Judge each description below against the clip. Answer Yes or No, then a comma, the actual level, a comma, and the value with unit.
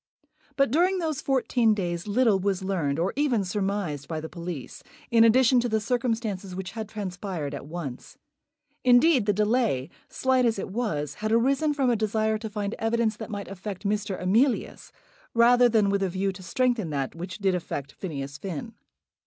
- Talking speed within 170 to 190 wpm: Yes, average, 180 wpm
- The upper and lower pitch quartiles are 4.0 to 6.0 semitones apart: Yes, average, 4.6 semitones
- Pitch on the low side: No, high, 210 Hz